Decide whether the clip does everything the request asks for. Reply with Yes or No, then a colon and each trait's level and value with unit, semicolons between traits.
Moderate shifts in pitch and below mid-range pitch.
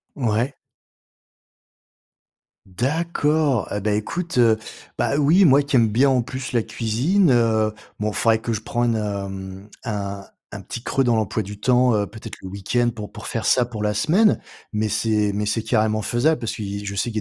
Yes: average, 3.5 semitones; low, 115 Hz